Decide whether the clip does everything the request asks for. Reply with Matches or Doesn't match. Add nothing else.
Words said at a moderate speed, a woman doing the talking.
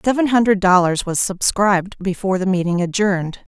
Matches